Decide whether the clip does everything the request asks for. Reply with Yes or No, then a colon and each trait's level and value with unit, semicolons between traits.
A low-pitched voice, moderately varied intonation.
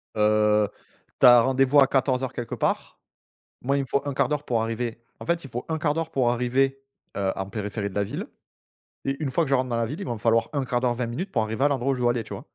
Yes: low, 125 Hz; average, 3.1 semitones